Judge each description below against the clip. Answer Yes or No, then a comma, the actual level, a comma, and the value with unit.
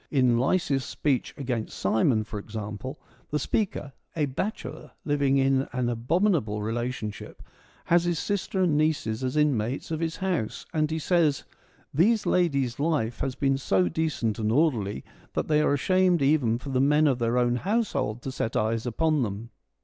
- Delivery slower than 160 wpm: No, average, 175 wpm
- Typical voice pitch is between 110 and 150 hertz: Yes, low, 135 Hz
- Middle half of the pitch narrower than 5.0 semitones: No, average, 5.3 semitones